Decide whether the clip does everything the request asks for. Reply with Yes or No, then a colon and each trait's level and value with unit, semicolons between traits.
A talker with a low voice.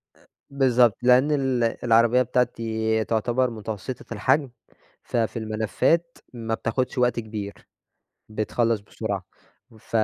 Yes: low, 115 Hz